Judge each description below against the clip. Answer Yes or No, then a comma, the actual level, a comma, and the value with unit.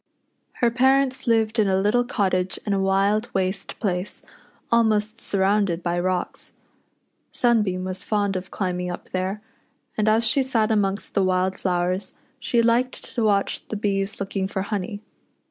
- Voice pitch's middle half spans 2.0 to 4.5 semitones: Yes, average, 2.9 semitones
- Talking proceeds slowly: No, average, 155 wpm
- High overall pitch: Yes, high, 200 Hz